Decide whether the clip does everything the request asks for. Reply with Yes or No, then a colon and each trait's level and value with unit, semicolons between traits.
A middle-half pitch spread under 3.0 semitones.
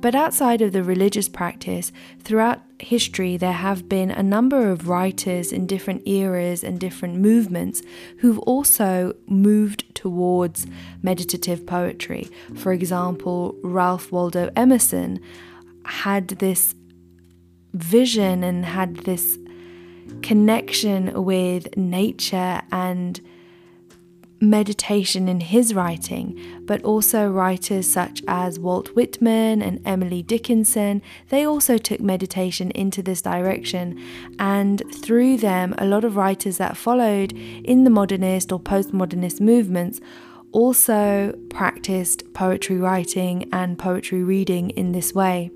Yes: narrow, 2.6 semitones